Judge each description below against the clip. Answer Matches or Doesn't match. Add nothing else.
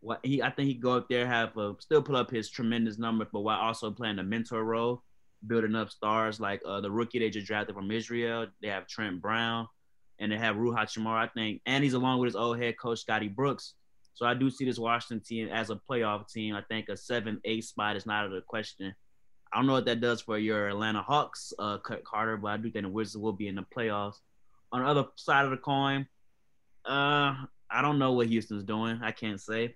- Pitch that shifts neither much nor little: Doesn't match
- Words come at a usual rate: Doesn't match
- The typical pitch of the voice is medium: Doesn't match